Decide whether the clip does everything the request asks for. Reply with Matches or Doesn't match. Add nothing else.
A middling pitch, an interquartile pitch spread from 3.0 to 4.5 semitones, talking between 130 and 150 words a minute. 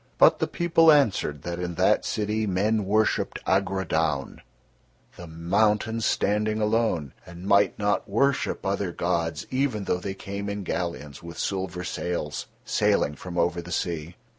Doesn't match